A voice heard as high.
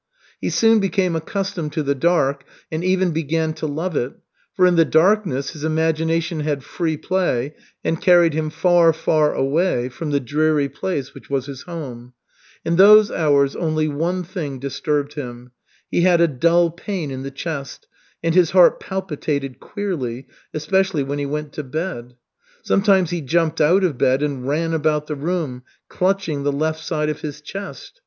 No: medium, 155 Hz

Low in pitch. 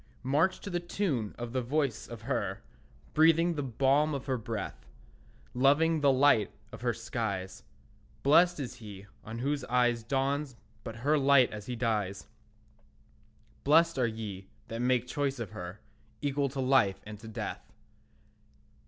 Yes: low, 125 Hz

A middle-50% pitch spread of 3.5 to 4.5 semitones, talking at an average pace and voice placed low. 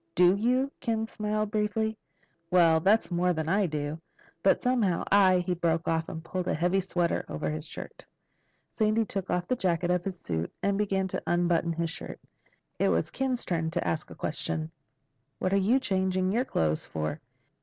No: average, 4.1 semitones; average, 185 wpm; medium, 180 Hz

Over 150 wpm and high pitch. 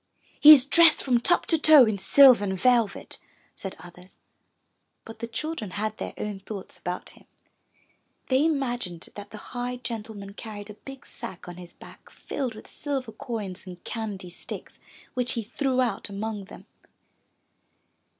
Yes: average, 160 wpm; high, 225 Hz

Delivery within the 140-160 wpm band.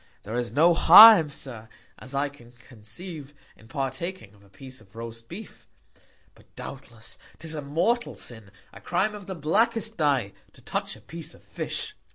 No: average, 175 wpm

